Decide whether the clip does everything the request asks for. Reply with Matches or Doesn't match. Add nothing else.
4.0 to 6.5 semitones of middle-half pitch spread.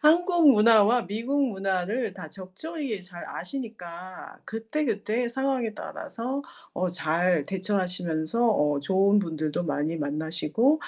Matches